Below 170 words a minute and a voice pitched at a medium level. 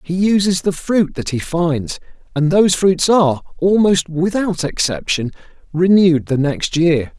Yes: average, 150 wpm; medium, 170 Hz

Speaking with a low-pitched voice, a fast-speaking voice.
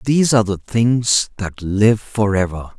No: low, 105 Hz; average, 170 wpm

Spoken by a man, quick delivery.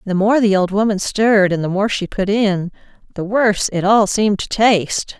No: female; fast, 220 wpm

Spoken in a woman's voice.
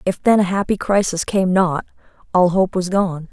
Yes: female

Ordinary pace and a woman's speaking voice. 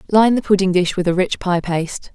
No: fast, 250 wpm; female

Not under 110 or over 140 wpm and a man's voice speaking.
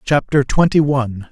Yes: slow, 135 wpm; male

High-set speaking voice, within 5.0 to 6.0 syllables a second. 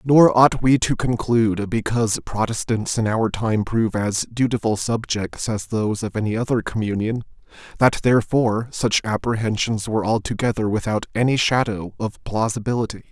No: low, 110 Hz; 5.2 syllables/s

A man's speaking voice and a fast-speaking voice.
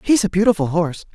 Yes: male; fast, 210 wpm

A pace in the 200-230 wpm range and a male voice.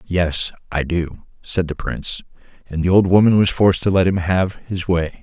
Yes: fast, 205 wpm; male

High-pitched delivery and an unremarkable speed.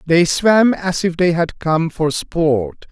No: medium, 165 Hz; average, 185 wpm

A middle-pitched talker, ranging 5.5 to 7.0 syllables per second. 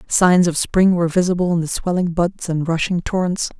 No: medium, 175 Hz; 5.3 syllables/s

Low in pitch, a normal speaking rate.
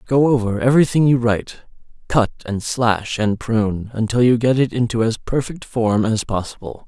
Yes: low, 115 Hz; average, 175 wpm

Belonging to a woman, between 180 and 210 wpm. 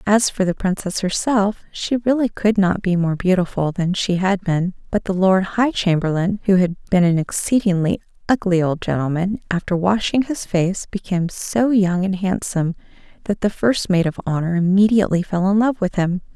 Yes: female; average, 185 wpm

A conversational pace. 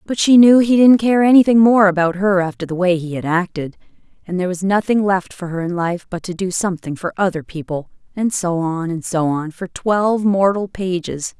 No: fast, 220 wpm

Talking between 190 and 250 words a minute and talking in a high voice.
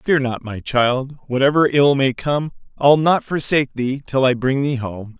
No: average, 195 wpm; low, 135 Hz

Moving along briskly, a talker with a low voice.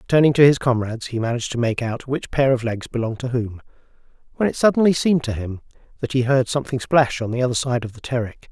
Yes: fast, 240 wpm; low, 125 Hz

